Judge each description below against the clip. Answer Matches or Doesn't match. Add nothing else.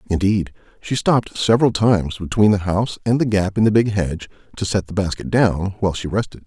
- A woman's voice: Doesn't match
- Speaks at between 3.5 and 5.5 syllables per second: Doesn't match